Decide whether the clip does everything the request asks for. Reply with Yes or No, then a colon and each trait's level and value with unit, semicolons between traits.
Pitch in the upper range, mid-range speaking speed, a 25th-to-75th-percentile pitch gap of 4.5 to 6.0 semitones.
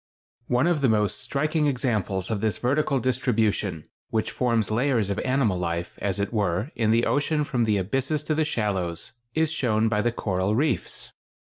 No: low, 115 Hz; average, 185 wpm; average, 5.0 semitones